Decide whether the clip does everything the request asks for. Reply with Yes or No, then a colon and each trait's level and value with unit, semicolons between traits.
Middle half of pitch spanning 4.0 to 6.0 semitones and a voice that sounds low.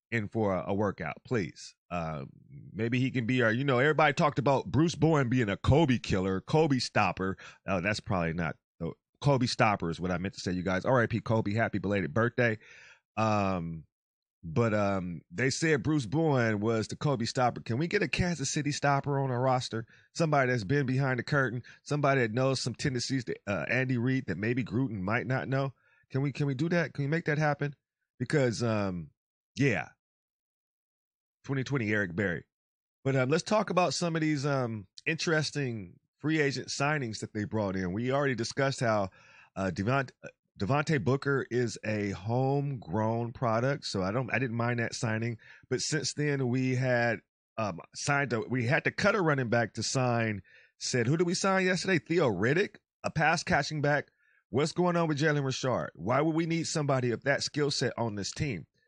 Yes: average, 4.7 semitones; low, 130 Hz